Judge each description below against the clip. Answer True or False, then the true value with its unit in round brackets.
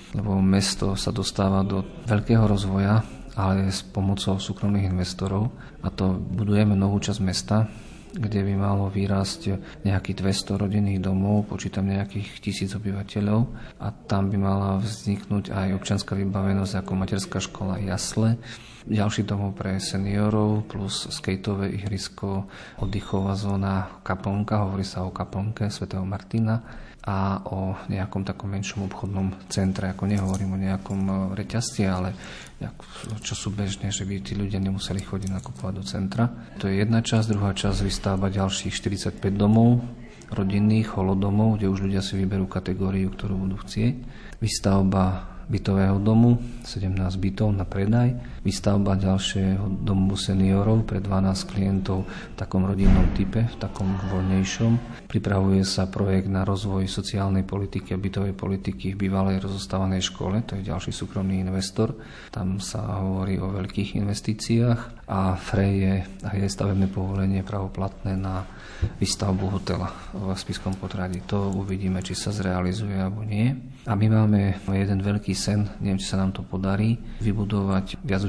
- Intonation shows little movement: True (1.3 semitones)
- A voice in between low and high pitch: False (95 Hz)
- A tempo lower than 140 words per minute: False (145 wpm)